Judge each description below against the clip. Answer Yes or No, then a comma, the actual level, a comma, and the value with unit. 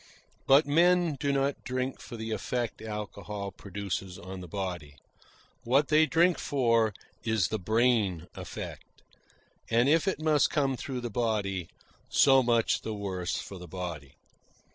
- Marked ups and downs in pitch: Yes, wide, 5.9 semitones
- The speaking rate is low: No, average, 145 wpm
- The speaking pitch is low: Yes, low, 115 Hz